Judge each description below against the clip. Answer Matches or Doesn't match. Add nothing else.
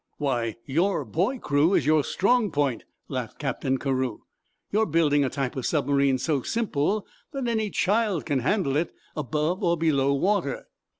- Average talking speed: Matches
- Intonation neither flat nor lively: Doesn't match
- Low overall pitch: Doesn't match